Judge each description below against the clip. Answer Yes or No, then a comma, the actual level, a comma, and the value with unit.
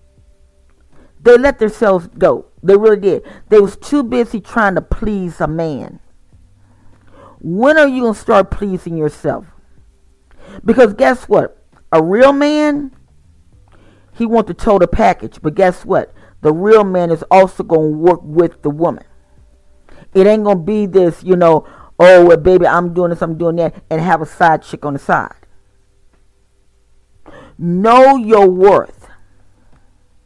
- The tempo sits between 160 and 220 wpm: No, average, 145 wpm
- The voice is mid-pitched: Yes, medium, 170 Hz